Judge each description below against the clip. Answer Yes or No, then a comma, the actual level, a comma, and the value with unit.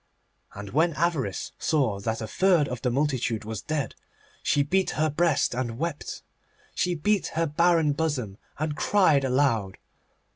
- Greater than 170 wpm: No, average, 150 wpm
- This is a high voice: No, medium, 145 Hz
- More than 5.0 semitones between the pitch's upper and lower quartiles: Yes, wide, 5.4 semitones